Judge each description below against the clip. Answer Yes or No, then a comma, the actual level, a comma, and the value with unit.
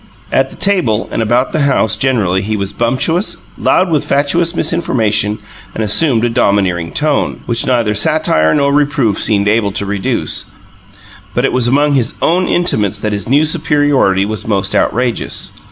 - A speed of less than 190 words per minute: Yes, average, 165 wpm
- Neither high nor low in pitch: No, low, 120 Hz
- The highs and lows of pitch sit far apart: Yes, wide, 5.9 semitones